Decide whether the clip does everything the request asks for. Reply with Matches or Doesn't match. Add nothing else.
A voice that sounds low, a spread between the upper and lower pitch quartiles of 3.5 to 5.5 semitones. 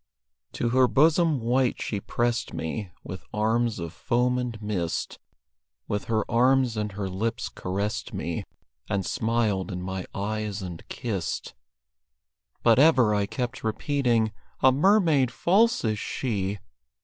Matches